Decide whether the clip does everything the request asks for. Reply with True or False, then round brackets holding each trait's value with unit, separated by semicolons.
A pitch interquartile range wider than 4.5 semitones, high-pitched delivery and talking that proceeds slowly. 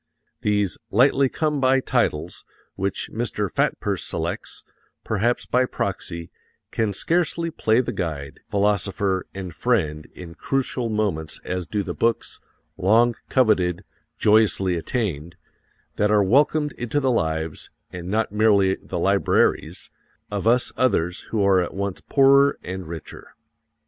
False (5.1 semitones; 105 Hz; 130 wpm)